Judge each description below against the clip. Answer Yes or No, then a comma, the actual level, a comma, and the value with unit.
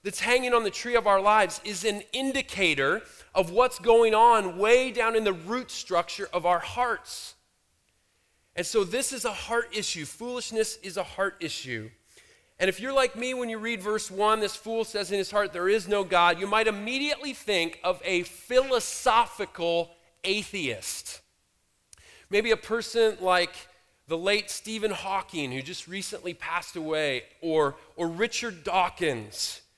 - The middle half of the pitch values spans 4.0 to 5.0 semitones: Yes, average, 4.4 semitones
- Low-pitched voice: No, high, 205 Hz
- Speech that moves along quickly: No, average, 165 wpm